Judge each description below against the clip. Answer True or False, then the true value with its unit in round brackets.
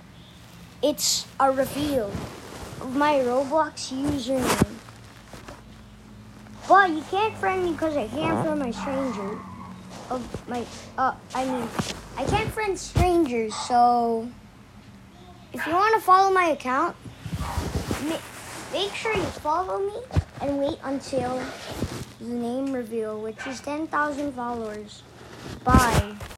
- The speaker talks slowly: True (115 wpm)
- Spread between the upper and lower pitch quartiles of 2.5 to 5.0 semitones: False (5.6 semitones)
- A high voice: True (265 Hz)